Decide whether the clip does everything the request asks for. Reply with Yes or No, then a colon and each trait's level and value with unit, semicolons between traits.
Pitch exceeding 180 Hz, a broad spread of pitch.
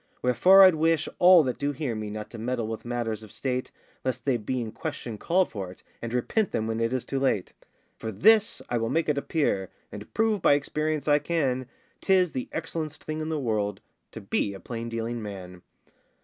No: low, 125 Hz; wide, 5.8 semitones